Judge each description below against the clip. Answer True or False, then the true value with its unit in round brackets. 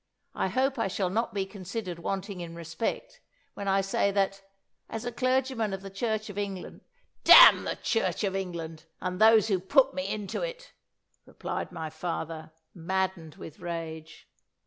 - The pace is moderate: True (170 wpm)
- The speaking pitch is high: True (195 Hz)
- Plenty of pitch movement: False (4.3 semitones)